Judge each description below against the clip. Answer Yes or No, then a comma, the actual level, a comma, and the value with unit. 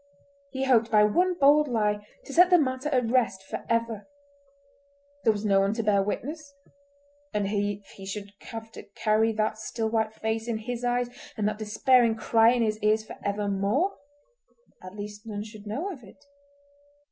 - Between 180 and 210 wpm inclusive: No, average, 170 wpm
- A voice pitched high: Yes, high, 225 Hz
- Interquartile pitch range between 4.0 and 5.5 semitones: Yes, average, 4.3 semitones